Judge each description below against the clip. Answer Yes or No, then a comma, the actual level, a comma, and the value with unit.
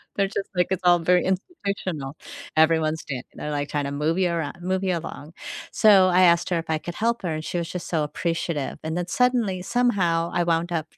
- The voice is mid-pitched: Yes, medium, 170 Hz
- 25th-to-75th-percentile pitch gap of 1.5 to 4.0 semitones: Yes, average, 2.7 semitones